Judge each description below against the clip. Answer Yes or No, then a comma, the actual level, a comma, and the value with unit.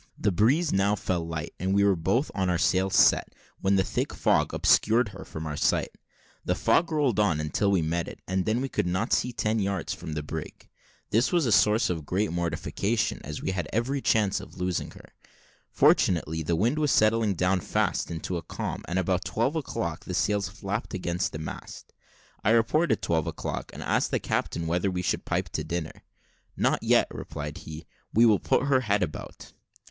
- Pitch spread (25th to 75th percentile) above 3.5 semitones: Yes, average, 4.7 semitones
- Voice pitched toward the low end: Yes, very low, 95 Hz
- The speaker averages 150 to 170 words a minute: No, average, 200 wpm